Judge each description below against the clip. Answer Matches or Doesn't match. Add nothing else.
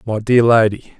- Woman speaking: Doesn't match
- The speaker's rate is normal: Matches